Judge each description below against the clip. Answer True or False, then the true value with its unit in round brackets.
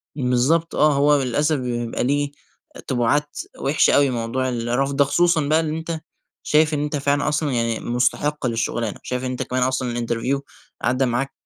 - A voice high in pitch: False (135 Hz)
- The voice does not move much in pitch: False (3.3 semitones)